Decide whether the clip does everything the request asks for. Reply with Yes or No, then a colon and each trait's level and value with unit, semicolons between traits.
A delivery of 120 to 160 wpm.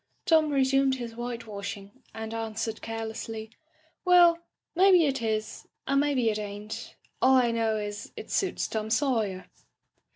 Yes: average, 150 wpm